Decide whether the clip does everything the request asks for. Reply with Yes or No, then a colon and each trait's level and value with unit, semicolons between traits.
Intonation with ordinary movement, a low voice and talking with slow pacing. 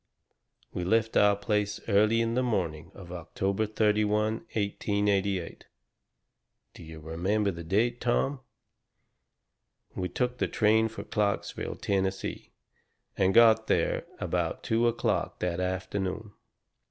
Yes: average, 3.0 semitones; low, 105 Hz; slow, 115 wpm